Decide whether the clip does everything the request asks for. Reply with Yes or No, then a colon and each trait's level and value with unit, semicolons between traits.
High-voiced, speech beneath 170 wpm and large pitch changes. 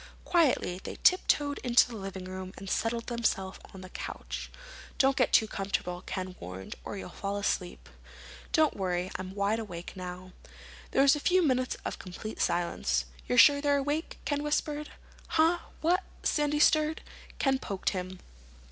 Yes: high, 215 Hz; average, 160 wpm; wide, 7.7 semitones